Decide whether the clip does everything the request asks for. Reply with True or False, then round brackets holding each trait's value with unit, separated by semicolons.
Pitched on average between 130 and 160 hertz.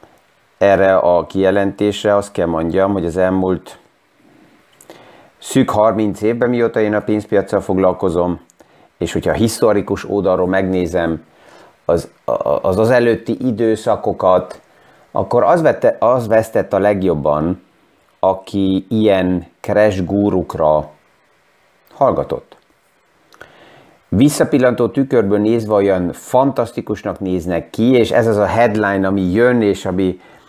False (100 Hz)